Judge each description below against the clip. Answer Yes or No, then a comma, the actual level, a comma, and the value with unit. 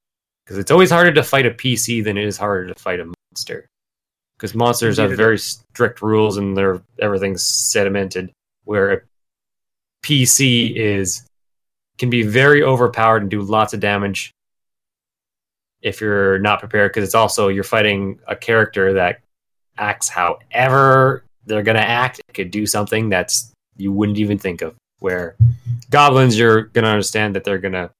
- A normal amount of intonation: Yes, average, 3.0 semitones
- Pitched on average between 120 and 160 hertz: No, low, 110 Hz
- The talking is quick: No, average, 160 wpm